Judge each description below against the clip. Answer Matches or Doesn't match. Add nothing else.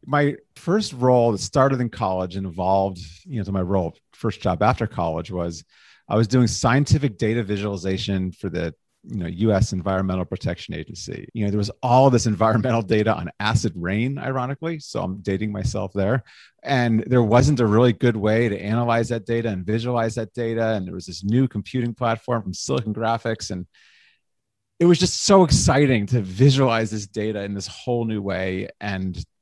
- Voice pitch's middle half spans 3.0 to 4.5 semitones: Matches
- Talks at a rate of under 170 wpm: Doesn't match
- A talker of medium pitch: Doesn't match